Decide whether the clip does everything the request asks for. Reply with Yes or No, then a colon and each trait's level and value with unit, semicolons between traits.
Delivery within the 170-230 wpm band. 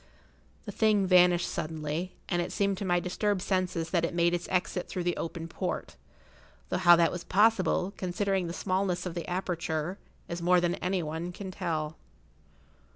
Yes: average, 175 wpm